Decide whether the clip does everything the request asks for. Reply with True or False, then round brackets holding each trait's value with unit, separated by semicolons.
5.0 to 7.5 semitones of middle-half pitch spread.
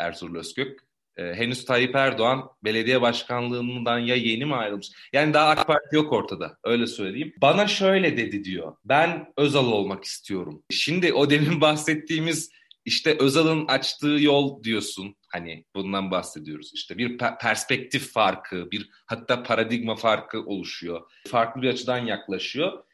True (5.6 semitones)